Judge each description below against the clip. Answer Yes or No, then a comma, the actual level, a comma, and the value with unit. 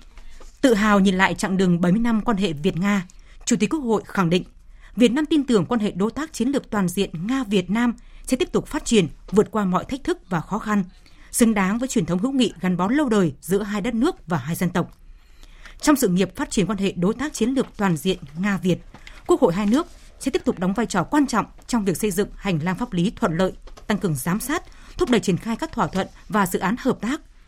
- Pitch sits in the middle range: No, high, 210 Hz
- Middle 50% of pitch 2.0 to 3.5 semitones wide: No, average, 4.5 semitones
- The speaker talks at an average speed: No, fast, 260 wpm